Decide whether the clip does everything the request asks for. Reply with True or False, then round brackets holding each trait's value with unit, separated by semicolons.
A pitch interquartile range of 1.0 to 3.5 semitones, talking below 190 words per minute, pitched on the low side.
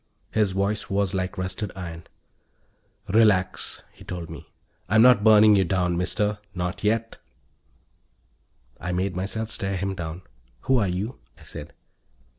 True (2.7 semitones; 140 wpm; 95 Hz)